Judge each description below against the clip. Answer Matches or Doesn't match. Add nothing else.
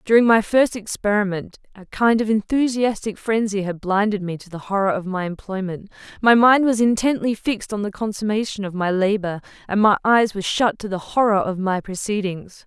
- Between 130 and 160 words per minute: Doesn't match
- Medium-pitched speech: Doesn't match